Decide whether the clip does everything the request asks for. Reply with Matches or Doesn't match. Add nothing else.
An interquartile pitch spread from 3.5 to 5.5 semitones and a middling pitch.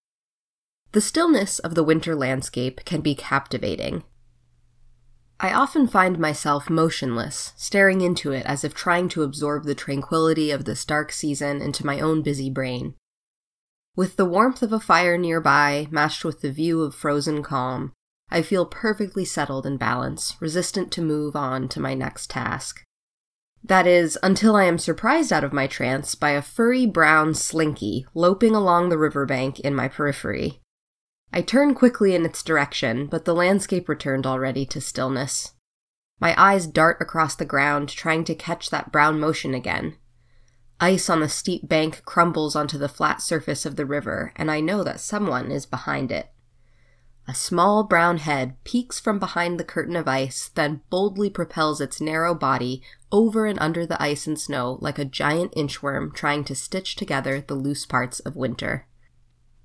Matches